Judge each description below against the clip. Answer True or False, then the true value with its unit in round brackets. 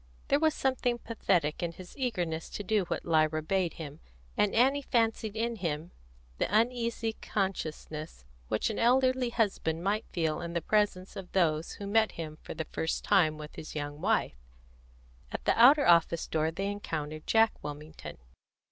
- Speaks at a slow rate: False (165 wpm)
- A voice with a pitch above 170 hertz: True (185 Hz)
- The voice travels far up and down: True (6.1 semitones)